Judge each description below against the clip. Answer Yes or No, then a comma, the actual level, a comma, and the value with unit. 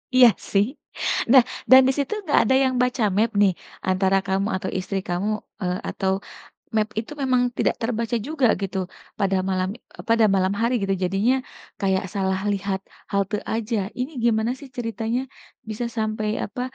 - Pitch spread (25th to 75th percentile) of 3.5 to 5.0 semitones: Yes, average, 3.9 semitones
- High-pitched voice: Yes, high, 215 Hz